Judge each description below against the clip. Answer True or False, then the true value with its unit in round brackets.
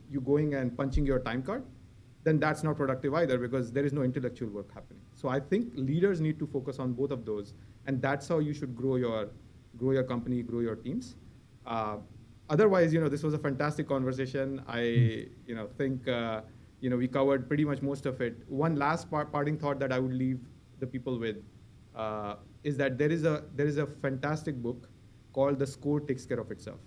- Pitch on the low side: True (130 Hz)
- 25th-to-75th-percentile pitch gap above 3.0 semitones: True (3.4 semitones)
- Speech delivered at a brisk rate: True (215 wpm)